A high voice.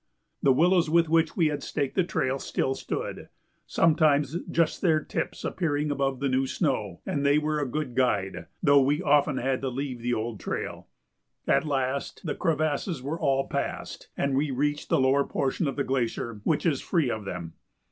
No: medium, 140 Hz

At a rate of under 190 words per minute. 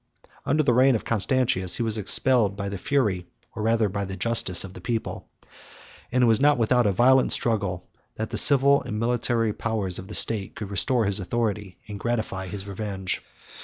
No: average, 195 wpm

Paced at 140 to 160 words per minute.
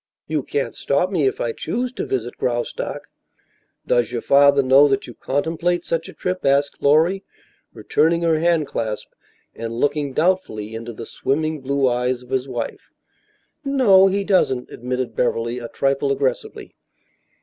Yes: average, 150 wpm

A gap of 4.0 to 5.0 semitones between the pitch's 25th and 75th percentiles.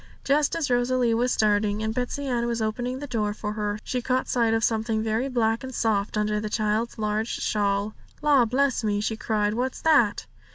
No: average, 2.8 semitones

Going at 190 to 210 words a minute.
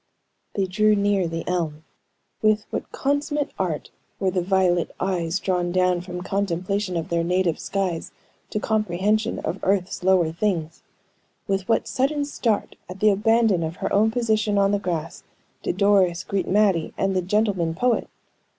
No: average, 160 wpm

